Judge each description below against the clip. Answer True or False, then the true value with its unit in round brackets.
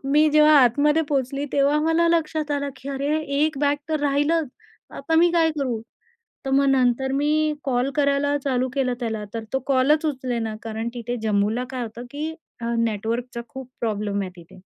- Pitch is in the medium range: False (275 Hz)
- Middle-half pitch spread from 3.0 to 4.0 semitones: True (3.7 semitones)